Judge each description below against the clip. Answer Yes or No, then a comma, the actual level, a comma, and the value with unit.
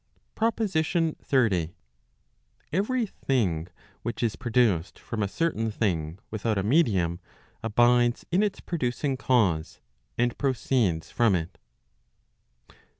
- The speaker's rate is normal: No, slow, 105 wpm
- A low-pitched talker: Yes, low, 120 Hz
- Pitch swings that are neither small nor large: No, wide, 6.3 semitones